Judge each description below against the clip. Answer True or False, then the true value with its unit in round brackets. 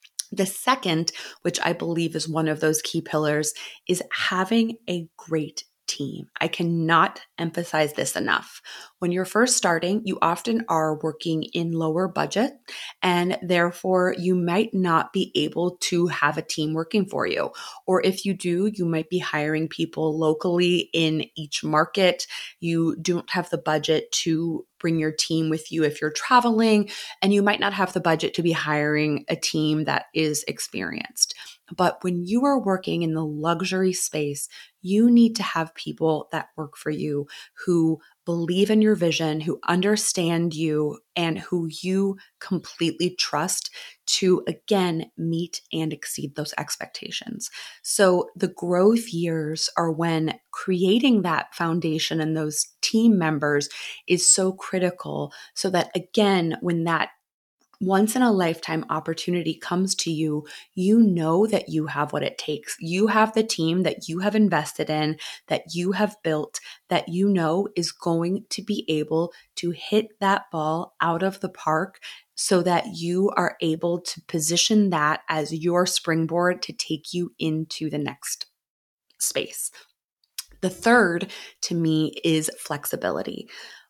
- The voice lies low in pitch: False (170 Hz)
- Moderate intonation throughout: True (3.1 semitones)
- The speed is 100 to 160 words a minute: True (155 wpm)